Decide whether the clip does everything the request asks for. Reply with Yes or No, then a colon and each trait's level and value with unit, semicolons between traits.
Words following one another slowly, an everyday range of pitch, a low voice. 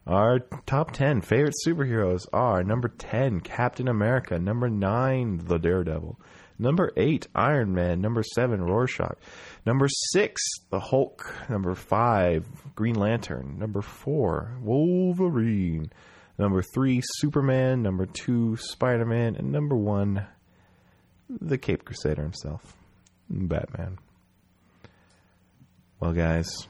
No: slow, 110 wpm; wide, 5.8 semitones; low, 110 Hz